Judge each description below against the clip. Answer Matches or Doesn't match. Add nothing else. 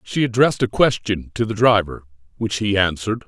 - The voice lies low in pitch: Matches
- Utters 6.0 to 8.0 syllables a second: Doesn't match